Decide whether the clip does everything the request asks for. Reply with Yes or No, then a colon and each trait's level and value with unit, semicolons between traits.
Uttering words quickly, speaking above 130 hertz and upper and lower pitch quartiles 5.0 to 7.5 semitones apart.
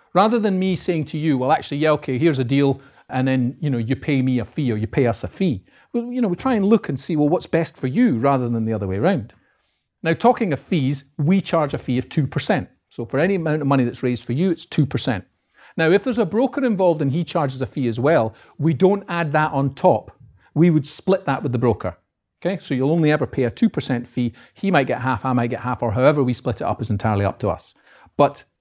Yes: fast, 260 wpm; medium, 140 Hz; wide, 5.5 semitones